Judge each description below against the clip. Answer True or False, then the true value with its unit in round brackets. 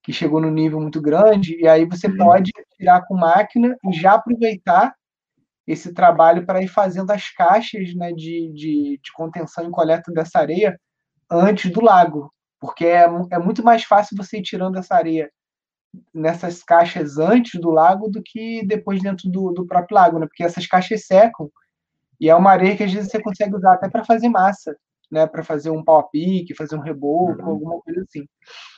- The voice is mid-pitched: True (180 Hz)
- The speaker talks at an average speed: False (190 wpm)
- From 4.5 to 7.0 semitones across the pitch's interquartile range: False (4.1 semitones)